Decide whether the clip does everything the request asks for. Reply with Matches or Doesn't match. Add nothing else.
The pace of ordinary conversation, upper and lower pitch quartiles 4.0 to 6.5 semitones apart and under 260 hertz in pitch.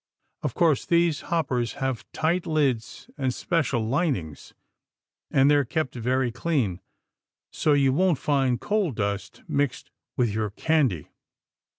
Doesn't match